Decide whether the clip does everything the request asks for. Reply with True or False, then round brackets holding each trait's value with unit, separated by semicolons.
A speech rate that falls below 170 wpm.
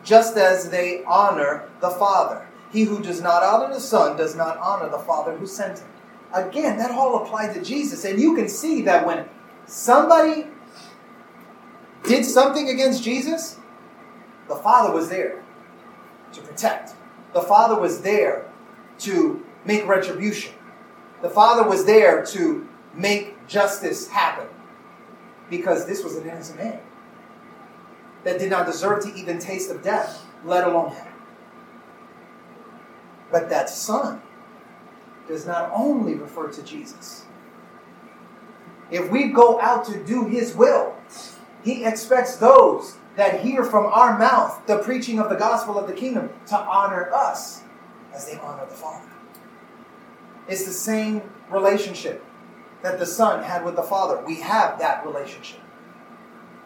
True (140 wpm)